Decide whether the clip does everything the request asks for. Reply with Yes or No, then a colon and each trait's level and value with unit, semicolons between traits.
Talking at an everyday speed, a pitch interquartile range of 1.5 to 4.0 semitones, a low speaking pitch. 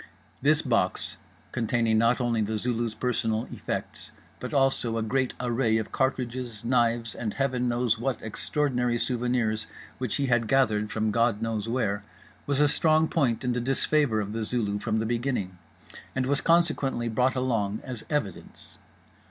Yes: average, 160 wpm; average, 2.8 semitones; low, 120 Hz